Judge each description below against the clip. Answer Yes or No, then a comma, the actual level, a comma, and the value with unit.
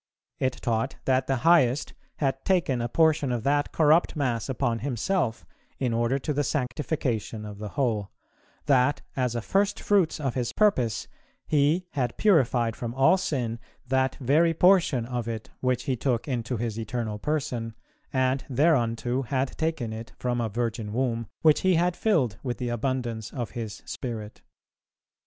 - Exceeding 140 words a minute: Yes, average, 160 wpm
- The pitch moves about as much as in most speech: Yes, average, 3.9 semitones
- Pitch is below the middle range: Yes, low, 130 Hz